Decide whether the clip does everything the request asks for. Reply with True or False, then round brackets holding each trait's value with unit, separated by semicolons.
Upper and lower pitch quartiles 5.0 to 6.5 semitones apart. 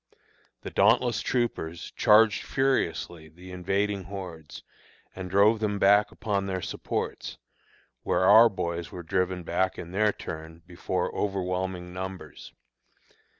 False (2.7 semitones)